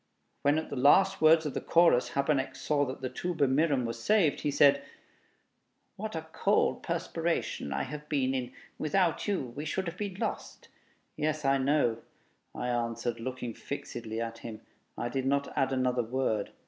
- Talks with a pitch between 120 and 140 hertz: Yes, low, 135 Hz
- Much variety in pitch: No, average, 3.9 semitones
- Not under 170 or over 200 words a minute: Yes, average, 175 wpm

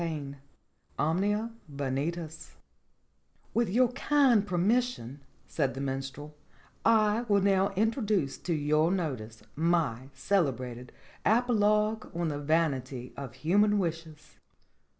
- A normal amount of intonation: No, wide, 7.1 semitones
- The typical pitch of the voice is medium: Yes, medium, 165 Hz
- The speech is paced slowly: Yes, slow, 105 wpm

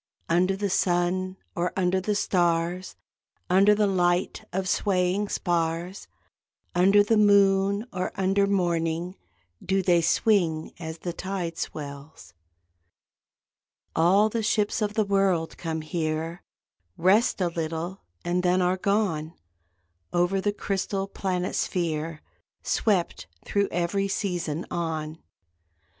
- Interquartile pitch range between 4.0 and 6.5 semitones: No, average, 2.8 semitones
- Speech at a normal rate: No, slow, 120 wpm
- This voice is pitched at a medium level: Yes, medium, 180 Hz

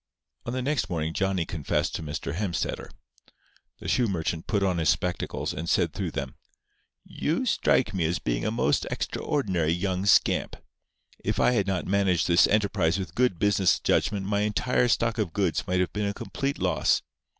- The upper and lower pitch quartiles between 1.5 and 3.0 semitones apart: No, average, 3.7 semitones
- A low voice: Yes, very low, 95 Hz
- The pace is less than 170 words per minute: No, average, 180 wpm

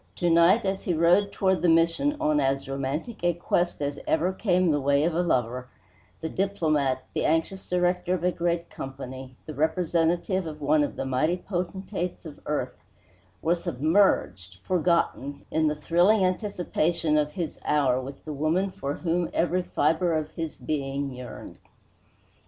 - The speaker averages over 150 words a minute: Yes, average, 165 wpm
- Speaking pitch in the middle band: Yes, medium, 165 Hz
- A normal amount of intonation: Yes, average, 3.8 semitones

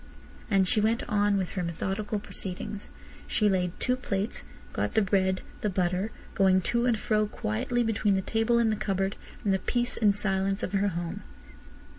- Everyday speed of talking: Yes, average, 180 wpm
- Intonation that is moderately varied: No, narrow, 2.3 semitones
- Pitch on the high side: Yes, high, 200 Hz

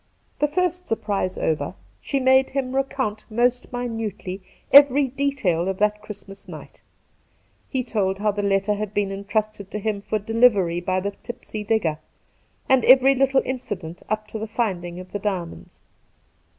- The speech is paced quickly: No, average, 155 wpm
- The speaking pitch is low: No, high, 215 Hz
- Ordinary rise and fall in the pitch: Yes, average, 4.4 semitones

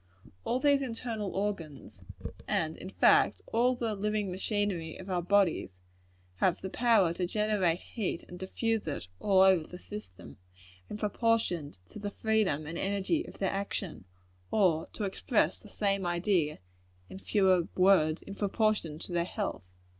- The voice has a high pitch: Yes, high, 195 Hz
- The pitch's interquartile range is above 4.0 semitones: No, average, 3.6 semitones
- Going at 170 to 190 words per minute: No, average, 150 wpm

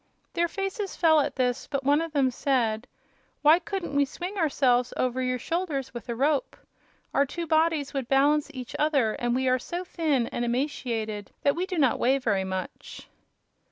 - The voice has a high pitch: Yes, very high, 275 Hz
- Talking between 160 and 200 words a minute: Yes, average, 185 wpm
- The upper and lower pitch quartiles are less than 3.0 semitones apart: No, average, 4.3 semitones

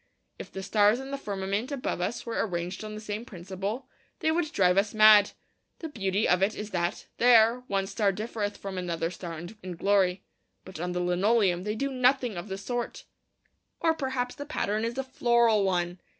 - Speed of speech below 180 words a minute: No, average, 195 wpm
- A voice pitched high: Yes, high, 205 Hz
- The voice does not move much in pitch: No, average, 4.2 semitones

